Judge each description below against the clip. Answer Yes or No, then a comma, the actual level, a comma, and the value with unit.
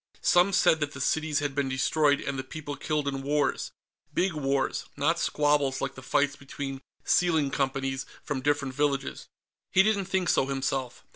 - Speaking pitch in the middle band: Yes, medium, 145 Hz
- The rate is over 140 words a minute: Yes, average, 170 wpm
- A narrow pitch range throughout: Yes, narrow, 2.1 semitones